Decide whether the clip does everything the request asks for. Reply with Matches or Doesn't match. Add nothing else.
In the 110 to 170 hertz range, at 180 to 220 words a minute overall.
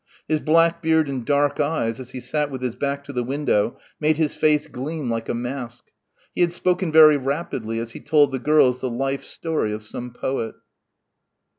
Matches